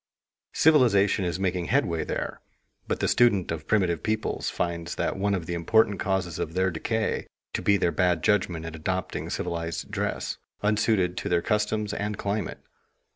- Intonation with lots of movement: No, average, 3.5 semitones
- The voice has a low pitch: Yes, very low, 95 Hz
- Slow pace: No, average, 160 wpm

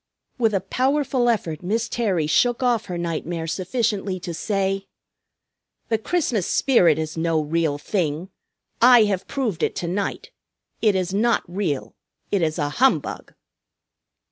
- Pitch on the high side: Yes, high, 195 Hz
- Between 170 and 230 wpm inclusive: No, average, 140 wpm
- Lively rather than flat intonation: Yes, wide, 5.7 semitones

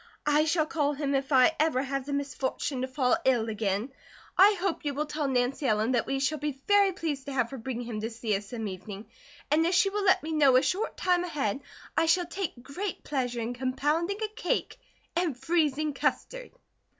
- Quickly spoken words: Yes, fast, 210 wpm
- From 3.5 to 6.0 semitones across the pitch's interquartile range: Yes, average, 4.7 semitones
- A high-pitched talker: Yes, very high, 280 Hz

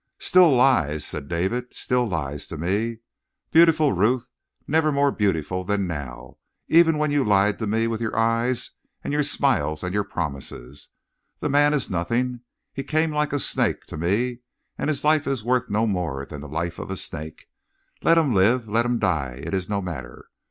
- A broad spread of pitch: Yes, wide, 8.0 semitones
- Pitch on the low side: Yes, low, 110 Hz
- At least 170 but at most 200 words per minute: Yes, average, 185 wpm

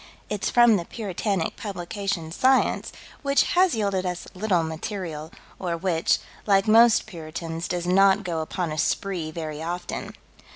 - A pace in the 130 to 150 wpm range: Yes, average, 140 wpm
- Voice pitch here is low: No, medium, 185 Hz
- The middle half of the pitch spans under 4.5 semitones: Yes, average, 3.9 semitones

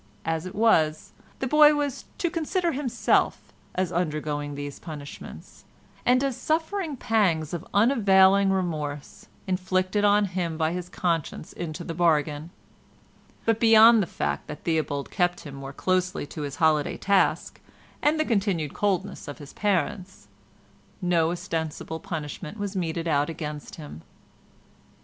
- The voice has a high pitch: No, medium, 180 Hz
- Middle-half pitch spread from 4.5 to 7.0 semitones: Yes, average, 4.9 semitones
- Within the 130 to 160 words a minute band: Yes, average, 140 wpm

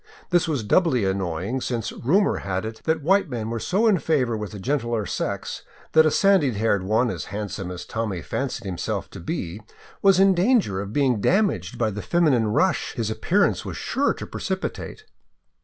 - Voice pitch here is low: Yes, low, 120 Hz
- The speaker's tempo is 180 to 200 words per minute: Yes, average, 190 wpm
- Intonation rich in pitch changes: Yes, wide, 8.9 semitones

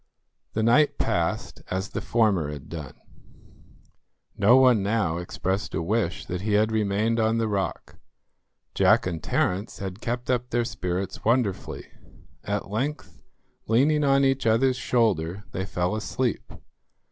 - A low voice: Yes, low, 110 Hz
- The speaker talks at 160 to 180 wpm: No, average, 140 wpm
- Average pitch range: Yes, average, 4.1 semitones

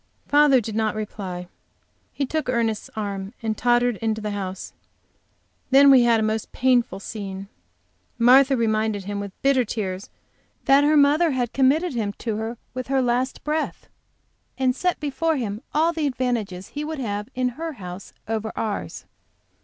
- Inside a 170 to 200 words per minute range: No, average, 160 wpm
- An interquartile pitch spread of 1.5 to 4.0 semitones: No, average, 4.4 semitones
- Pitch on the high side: Yes, high, 240 Hz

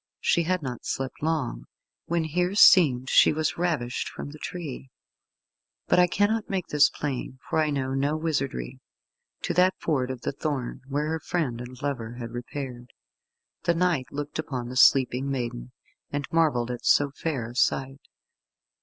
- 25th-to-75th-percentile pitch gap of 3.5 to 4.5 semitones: Yes, average, 4.2 semitones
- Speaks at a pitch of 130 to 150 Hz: Yes, medium, 140 Hz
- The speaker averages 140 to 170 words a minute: Yes, average, 165 wpm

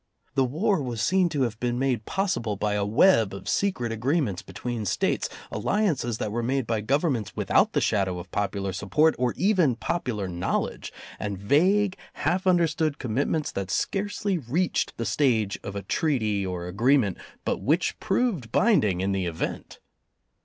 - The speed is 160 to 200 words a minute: Yes, average, 170 wpm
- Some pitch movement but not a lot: No, wide, 8.0 semitones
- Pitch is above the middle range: No, low, 120 Hz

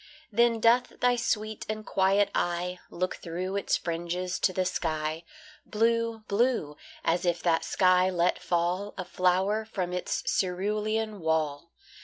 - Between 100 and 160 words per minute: Yes, average, 140 wpm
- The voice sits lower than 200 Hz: Yes, medium, 185 Hz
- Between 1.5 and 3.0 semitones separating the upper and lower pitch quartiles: No, average, 3.7 semitones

